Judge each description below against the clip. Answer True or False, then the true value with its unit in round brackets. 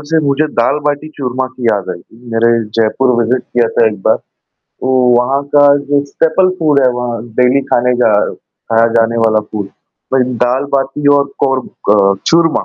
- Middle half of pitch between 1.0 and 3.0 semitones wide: False (3.6 semitones)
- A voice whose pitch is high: False (125 Hz)